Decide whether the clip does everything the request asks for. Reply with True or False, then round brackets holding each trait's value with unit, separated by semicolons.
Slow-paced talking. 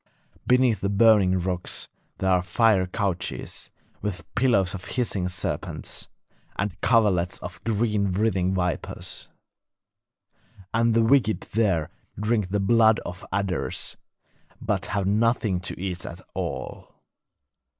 True (120 wpm)